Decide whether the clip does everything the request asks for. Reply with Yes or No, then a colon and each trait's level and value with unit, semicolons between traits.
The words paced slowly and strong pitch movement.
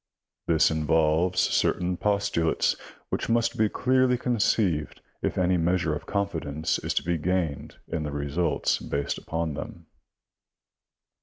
No: slow, 130 wpm; average, 4.3 semitones